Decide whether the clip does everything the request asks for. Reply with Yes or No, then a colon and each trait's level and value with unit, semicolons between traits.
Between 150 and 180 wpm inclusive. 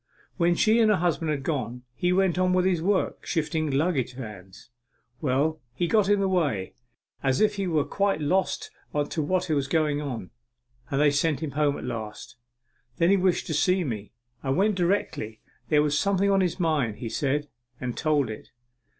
No: average, 190 wpm